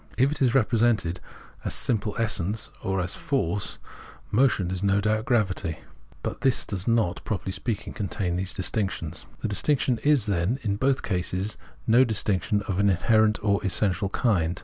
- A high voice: No, low, 105 Hz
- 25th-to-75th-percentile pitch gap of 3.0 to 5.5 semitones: Yes, average, 3.6 semitones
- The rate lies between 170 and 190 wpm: No, average, 160 wpm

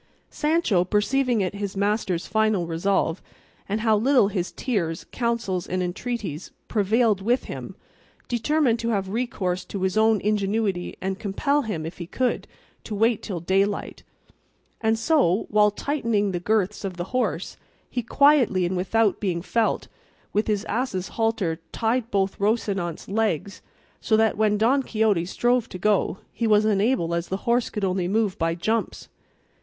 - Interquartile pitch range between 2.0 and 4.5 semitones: Yes, average, 3.5 semitones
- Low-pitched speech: No, high, 210 Hz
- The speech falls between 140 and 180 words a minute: Yes, average, 160 wpm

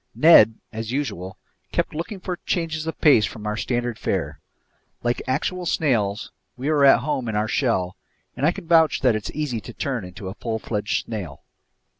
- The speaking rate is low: No, average, 185 wpm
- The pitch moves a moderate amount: No, wide, 6.2 semitones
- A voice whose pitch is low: Yes, low, 120 Hz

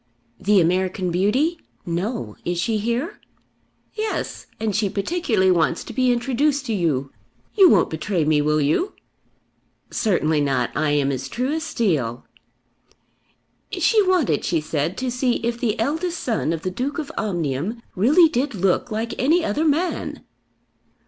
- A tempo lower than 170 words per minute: Yes, average, 150 wpm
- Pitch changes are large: Yes, wide, 8.5 semitones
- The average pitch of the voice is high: Yes, high, 215 Hz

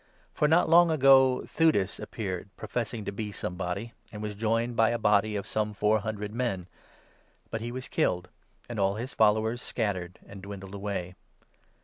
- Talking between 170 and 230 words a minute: Yes, average, 175 wpm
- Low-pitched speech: Yes, low, 110 Hz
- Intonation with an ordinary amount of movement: Yes, average, 3.0 semitones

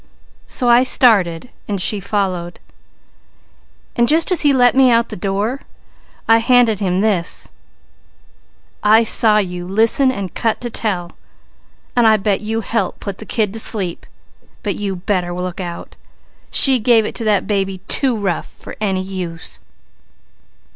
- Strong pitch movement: No, average, 3.6 semitones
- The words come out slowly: No, average, 155 wpm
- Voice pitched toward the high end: Yes, high, 210 Hz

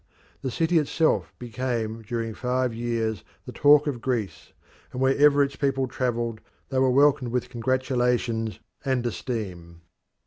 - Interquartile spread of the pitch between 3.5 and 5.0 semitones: No, average, 2.7 semitones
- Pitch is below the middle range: Yes, low, 125 Hz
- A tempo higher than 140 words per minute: No, slow, 135 wpm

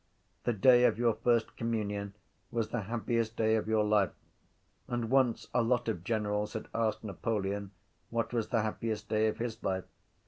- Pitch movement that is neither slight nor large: No, narrow, 1.8 semitones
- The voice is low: Yes, low, 110 Hz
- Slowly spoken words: No, average, 175 wpm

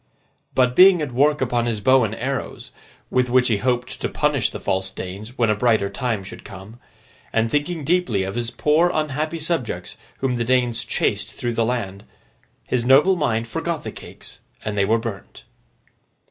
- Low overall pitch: Yes, low, 120 Hz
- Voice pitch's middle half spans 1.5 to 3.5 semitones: No, average, 4.0 semitones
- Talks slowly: No, average, 180 wpm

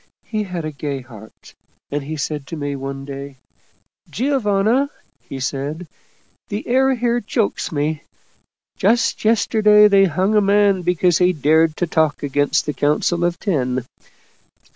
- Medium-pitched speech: Yes, medium, 170 Hz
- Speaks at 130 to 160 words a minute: Yes, average, 155 wpm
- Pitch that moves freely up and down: Yes, wide, 6.3 semitones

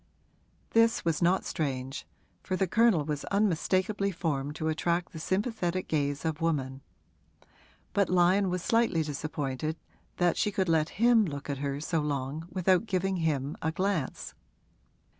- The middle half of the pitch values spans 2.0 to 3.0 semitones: No, average, 4.2 semitones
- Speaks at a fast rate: No, average, 145 wpm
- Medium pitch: Yes, medium, 165 Hz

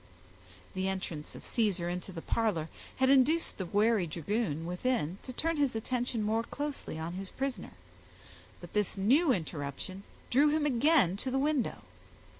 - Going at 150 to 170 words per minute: Yes, average, 155 wpm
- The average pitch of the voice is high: Yes, high, 215 Hz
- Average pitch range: No, wide, 6.7 semitones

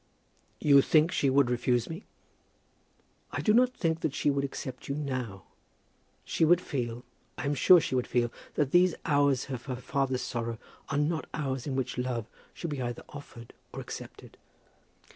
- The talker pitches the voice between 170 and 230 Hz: No, medium, 140 Hz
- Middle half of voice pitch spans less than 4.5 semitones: Yes, average, 3.4 semitones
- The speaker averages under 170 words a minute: No, average, 175 wpm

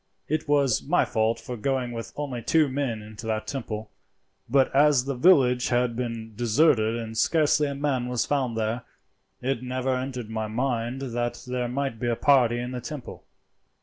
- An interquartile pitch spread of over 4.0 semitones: No, average, 3.0 semitones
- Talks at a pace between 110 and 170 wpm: No, average, 180 wpm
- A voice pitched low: Yes, low, 125 Hz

